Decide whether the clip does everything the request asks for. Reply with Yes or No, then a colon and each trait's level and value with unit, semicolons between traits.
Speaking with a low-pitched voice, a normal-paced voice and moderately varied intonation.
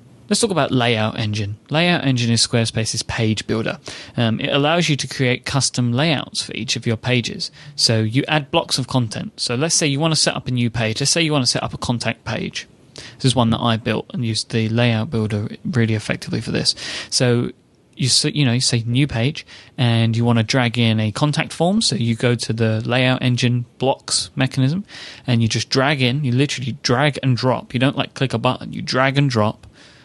No: low, 125 Hz; fast, 225 wpm; average, 3.4 semitones